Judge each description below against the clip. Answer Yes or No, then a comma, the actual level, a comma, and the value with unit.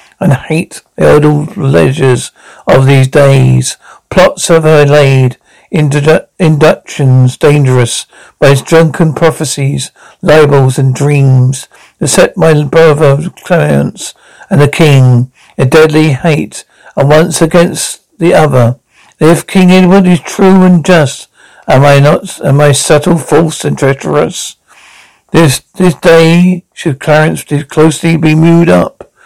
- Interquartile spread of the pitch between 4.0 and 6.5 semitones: No, average, 3.2 semitones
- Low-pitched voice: No, medium, 155 Hz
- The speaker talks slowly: Yes, slow, 130 wpm